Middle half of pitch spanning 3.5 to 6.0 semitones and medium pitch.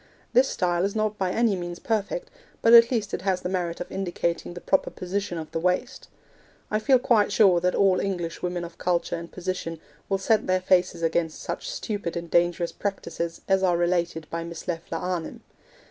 No: average, 2.8 semitones; medium, 180 Hz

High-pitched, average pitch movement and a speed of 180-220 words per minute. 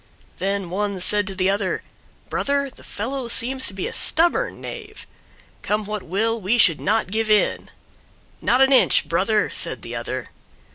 No: high, 210 Hz; average, 4.7 semitones; average, 170 wpm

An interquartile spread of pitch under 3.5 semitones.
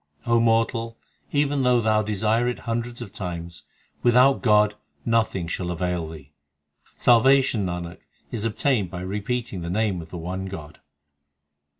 No: average, 4.8 semitones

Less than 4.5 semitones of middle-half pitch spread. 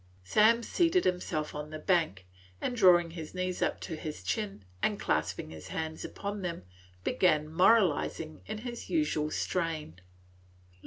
No: average, 5.0 semitones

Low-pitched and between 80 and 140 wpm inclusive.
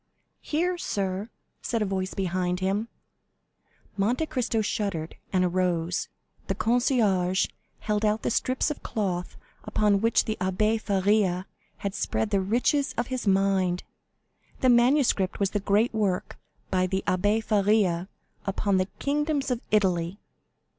No: high, 200 Hz; slow, 135 wpm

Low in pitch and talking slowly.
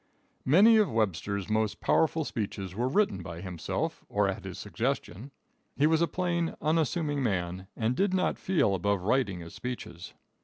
No: low, 115 Hz; average, 160 wpm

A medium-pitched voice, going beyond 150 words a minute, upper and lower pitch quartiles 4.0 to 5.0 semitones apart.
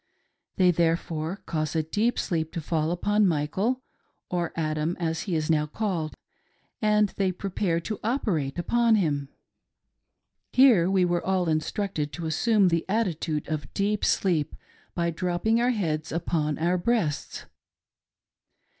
No: medium, 175 Hz; average, 145 wpm; average, 4.3 semitones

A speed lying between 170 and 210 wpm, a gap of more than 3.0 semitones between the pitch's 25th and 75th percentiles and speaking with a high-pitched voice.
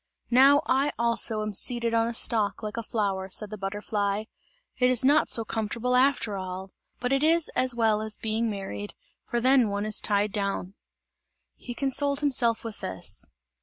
Yes: average, 175 wpm; average, 3.4 semitones; high, 225 Hz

